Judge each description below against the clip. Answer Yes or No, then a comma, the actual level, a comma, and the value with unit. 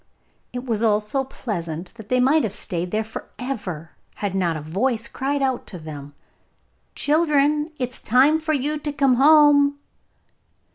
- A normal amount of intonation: No, wide, 6.5 semitones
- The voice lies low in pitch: No, very high, 250 Hz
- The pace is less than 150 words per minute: No, average, 165 wpm